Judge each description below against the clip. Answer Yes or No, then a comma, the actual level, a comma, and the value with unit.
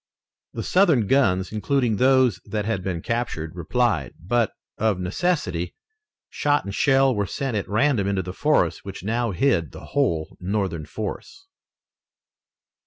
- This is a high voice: No, low, 105 Hz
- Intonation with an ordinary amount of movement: No, wide, 6.0 semitones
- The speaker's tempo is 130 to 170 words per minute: Yes, average, 140 wpm